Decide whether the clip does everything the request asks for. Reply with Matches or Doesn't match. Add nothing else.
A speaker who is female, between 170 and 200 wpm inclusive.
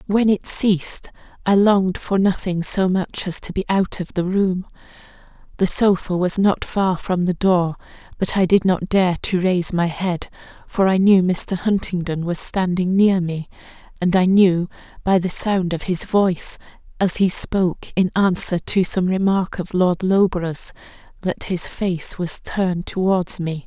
Matches